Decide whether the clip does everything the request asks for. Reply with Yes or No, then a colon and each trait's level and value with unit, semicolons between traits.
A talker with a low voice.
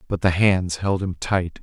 Yes: very low, 90 Hz